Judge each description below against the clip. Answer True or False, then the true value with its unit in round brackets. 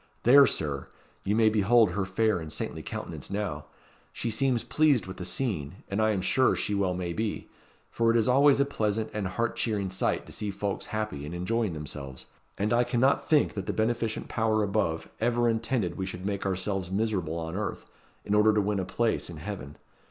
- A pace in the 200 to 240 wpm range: True (205 wpm)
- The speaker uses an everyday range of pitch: True (3.7 semitones)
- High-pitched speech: False (105 Hz)